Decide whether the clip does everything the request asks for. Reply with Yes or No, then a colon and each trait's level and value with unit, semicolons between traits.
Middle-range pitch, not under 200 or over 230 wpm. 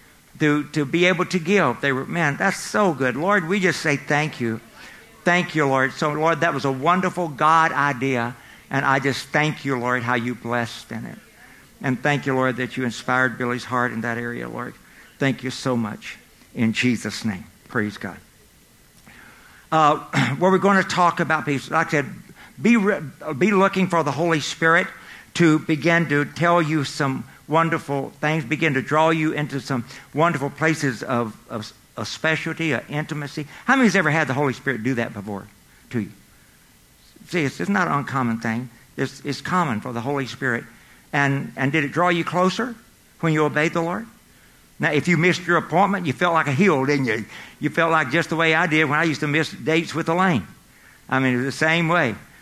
Yes: medium, 150 Hz; fast, 205 wpm